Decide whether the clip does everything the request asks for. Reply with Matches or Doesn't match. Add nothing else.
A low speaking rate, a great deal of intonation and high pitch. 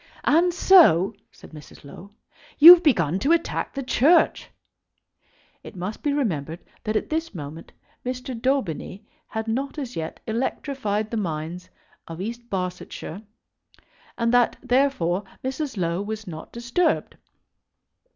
Matches